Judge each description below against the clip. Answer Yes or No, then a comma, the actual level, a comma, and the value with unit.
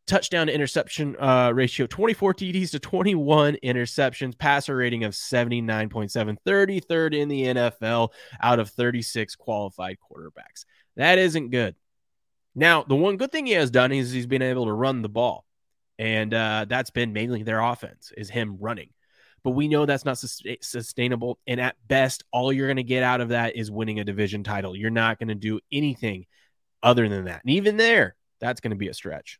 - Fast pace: No, average, 190 wpm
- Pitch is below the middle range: Yes, low, 125 Hz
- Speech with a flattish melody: No, average, 4.1 semitones